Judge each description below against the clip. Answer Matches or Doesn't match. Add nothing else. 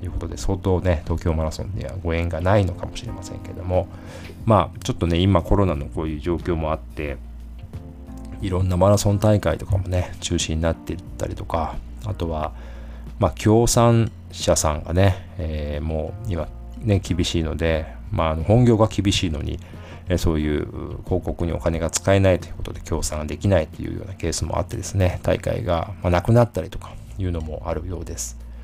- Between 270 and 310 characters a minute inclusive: Doesn't match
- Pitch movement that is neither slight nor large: Matches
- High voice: Doesn't match